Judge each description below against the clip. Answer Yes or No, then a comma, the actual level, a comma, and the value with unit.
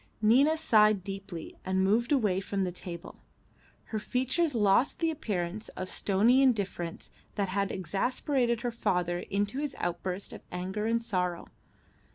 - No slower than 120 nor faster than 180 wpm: Yes, average, 145 wpm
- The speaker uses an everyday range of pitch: Yes, average, 4.2 semitones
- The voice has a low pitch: No, high, 205 Hz